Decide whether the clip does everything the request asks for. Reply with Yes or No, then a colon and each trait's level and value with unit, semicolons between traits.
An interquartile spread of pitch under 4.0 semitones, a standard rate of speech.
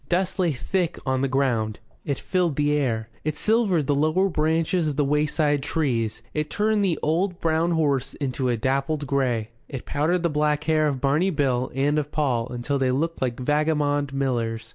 Yes: average, 3.4 semitones; average, 185 wpm